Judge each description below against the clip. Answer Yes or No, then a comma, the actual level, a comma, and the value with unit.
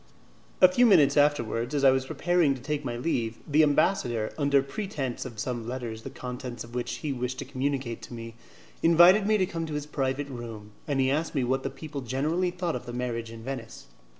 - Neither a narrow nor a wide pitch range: Yes, average, 4.0 semitones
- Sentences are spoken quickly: Yes, fast, 210 wpm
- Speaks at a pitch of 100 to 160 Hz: Yes, low, 135 Hz